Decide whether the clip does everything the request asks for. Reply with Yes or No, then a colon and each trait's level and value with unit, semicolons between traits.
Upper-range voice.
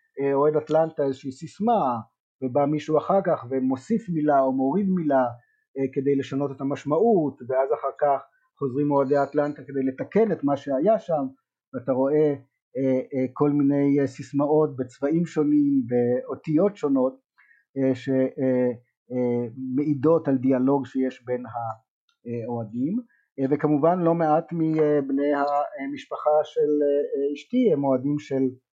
No: medium, 140 Hz